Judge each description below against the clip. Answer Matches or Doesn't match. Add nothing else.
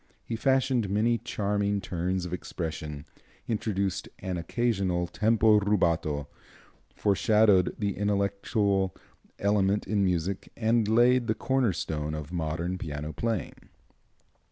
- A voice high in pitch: Doesn't match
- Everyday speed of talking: Doesn't match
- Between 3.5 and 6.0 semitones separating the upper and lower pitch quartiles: Matches